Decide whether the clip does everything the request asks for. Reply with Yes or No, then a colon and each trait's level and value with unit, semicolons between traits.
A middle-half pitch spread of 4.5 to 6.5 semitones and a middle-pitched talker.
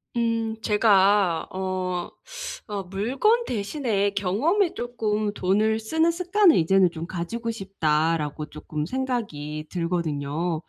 No: average, 5.3 semitones; high, 200 Hz